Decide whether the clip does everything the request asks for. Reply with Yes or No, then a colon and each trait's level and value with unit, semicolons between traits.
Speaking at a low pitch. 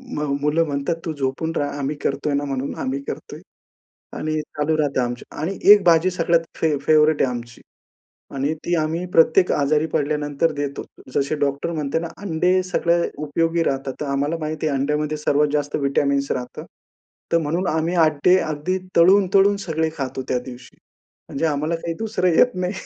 No: medium, 155 Hz